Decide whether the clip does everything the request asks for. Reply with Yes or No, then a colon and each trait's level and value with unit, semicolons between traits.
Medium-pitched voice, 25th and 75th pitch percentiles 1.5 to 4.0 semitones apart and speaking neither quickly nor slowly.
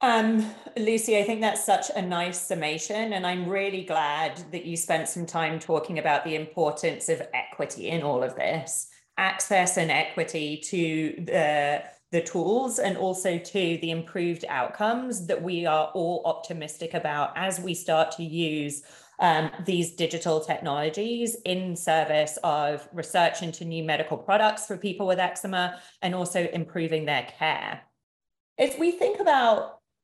Yes: medium, 175 Hz; average, 3.2 semitones; average, 155 wpm